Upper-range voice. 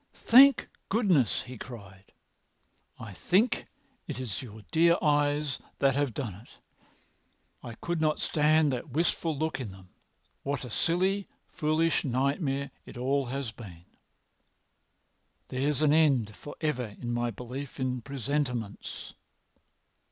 No: low, 135 Hz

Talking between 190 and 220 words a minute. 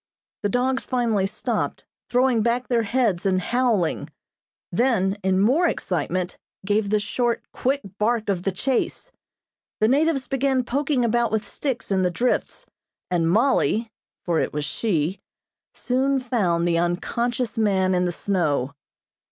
No: average, 145 wpm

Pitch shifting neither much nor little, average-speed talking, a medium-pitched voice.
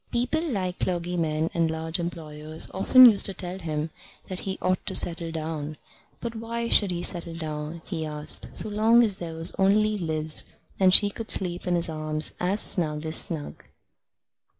Yes: average, 3.7 semitones; average, 175 wpm; medium, 175 Hz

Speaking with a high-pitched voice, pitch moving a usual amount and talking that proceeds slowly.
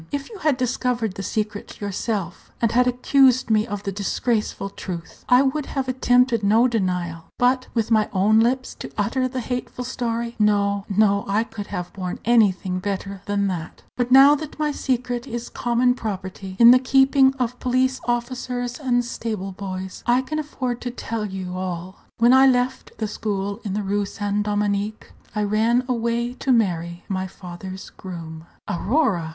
No: high, 225 Hz; average, 4.1 semitones; average, 170 wpm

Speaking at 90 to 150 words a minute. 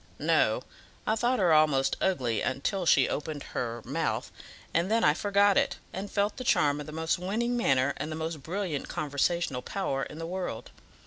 No: average, 185 wpm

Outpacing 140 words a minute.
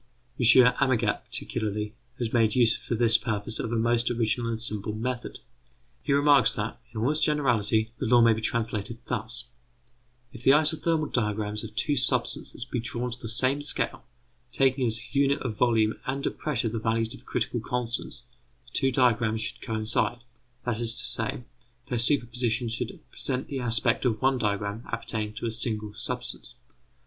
Yes: average, 175 wpm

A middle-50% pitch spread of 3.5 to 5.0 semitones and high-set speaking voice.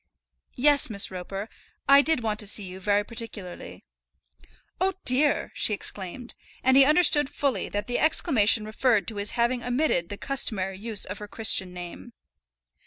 Yes: average, 4.5 semitones; high, 225 Hz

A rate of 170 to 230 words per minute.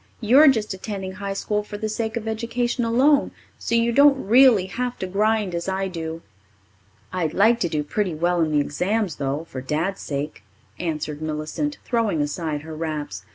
Yes: average, 180 wpm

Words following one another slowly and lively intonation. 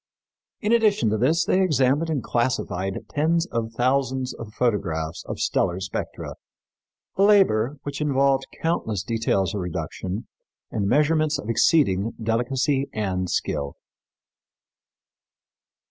Yes: slow, 115 wpm; wide, 6.4 semitones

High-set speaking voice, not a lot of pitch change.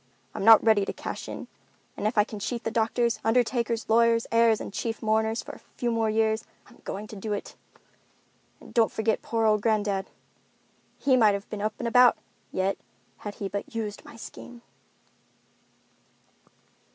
Yes: high, 220 Hz; narrow, 1.6 semitones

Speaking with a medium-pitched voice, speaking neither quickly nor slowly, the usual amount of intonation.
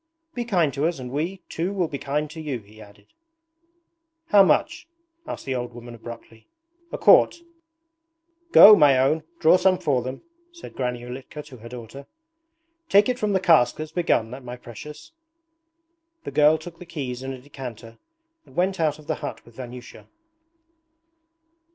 No: medium, 145 Hz; average, 170 wpm; wide, 5.7 semitones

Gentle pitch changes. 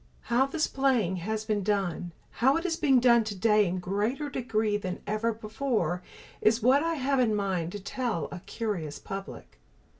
No: average, 4.7 semitones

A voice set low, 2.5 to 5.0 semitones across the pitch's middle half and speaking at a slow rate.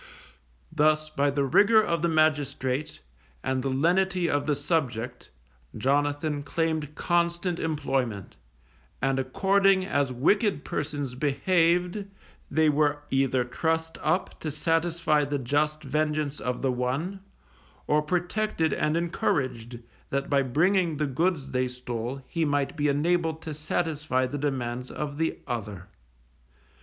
No: medium, 150 Hz; average, 3.4 semitones; slow, 130 wpm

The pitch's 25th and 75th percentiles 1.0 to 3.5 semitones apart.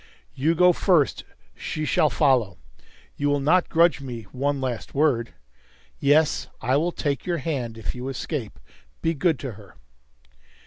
No: average, 4.0 semitones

